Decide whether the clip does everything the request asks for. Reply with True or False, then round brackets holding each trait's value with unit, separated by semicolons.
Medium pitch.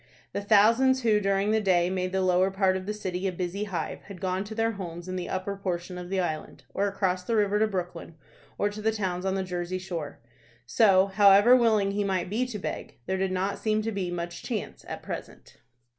False (195 Hz)